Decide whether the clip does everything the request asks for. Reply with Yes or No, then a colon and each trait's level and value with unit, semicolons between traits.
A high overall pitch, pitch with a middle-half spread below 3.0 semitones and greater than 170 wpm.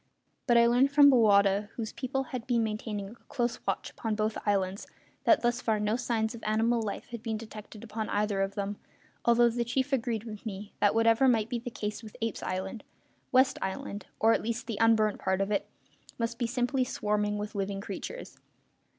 Yes: high, 225 Hz; narrow, 2.4 semitones; average, 200 wpm